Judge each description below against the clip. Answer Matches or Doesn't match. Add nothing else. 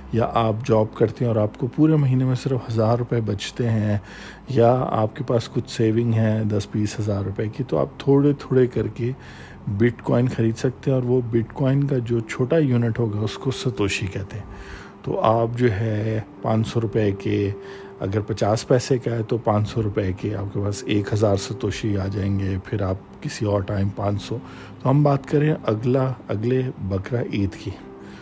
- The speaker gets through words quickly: Matches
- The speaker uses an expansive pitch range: Doesn't match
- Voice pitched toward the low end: Matches